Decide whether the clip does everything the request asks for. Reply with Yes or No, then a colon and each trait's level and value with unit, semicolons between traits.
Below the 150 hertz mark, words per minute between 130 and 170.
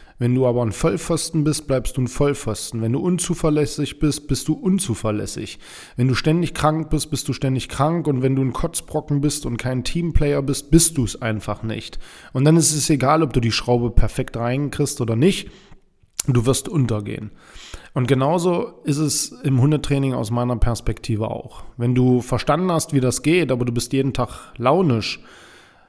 No: low, 135 Hz; average, 185 wpm